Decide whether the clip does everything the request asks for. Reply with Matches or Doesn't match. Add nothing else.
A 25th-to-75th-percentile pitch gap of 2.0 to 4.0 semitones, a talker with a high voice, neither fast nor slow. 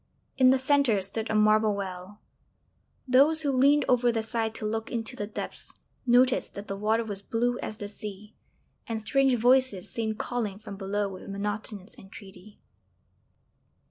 Matches